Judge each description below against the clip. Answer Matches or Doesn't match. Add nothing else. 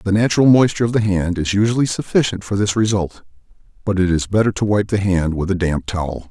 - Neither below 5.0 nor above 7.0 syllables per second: Matches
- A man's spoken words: Matches